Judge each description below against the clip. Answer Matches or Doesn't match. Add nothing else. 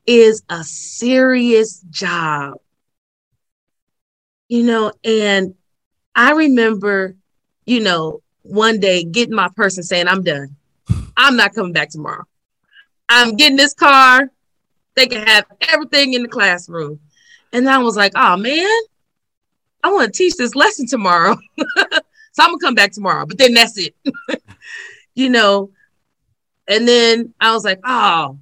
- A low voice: Doesn't match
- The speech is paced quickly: Doesn't match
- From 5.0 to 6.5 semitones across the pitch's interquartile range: Matches